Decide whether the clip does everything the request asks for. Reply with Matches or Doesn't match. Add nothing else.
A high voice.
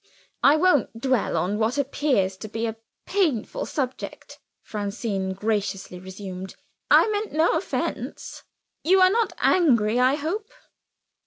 Matches